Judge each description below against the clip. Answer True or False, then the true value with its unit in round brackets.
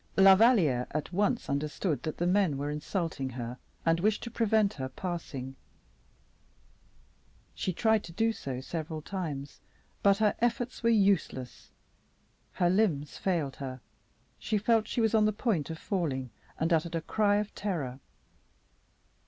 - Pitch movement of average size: False (6.4 semitones)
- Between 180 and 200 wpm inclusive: False (150 wpm)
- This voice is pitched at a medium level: True (175 Hz)